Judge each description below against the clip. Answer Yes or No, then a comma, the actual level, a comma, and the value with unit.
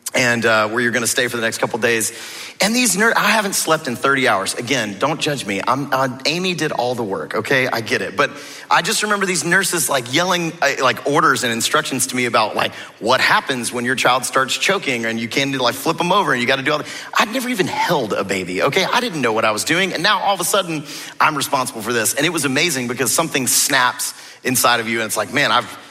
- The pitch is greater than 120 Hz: Yes, low, 135 Hz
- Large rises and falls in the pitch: Yes, wide, 5.7 semitones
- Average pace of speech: No, fast, 260 wpm